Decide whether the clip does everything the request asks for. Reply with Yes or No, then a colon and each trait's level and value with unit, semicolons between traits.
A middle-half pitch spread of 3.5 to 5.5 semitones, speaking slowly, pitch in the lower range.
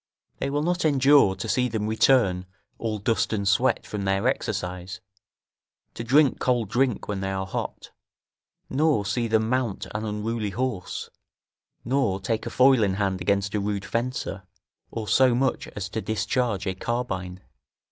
No: average, 4.5 semitones; average, 160 wpm; low, 110 Hz